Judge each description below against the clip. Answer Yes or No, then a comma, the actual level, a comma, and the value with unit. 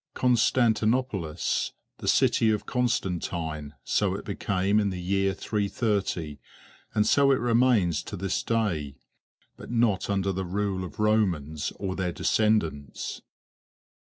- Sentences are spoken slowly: Yes, slow, 125 wpm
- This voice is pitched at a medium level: No, low, 100 Hz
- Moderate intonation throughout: Yes, average, 4.0 semitones